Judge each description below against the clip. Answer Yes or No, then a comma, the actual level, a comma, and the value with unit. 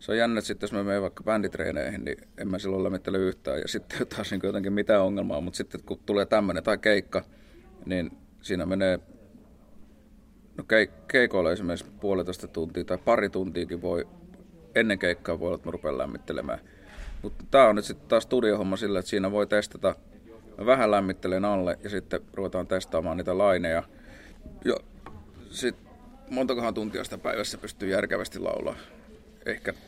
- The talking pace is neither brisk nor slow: No, fast, 165 wpm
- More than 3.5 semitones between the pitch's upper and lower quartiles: No, narrow, 2.4 semitones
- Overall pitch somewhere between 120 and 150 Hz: No, low, 100 Hz